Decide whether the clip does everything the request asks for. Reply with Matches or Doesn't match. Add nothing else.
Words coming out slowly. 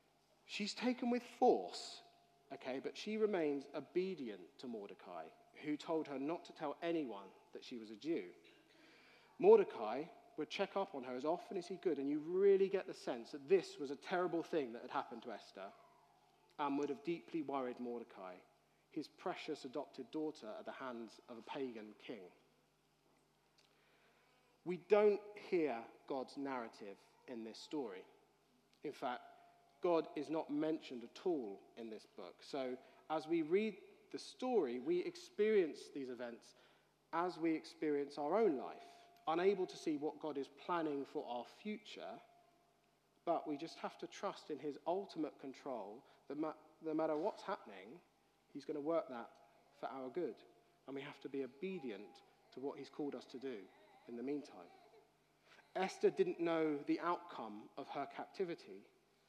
Doesn't match